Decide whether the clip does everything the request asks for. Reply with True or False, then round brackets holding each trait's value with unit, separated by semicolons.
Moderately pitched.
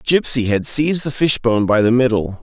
False (125 Hz)